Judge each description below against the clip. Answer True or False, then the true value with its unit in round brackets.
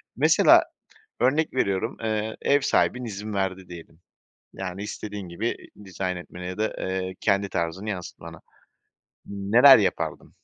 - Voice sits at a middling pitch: False (100 Hz)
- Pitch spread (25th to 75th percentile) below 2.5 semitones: False (2.9 semitones)